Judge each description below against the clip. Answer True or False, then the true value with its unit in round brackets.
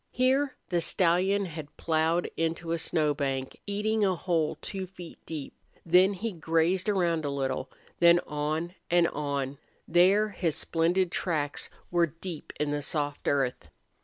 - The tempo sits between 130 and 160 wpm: True (155 wpm)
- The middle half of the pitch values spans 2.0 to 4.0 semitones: True (3.6 semitones)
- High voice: False (170 Hz)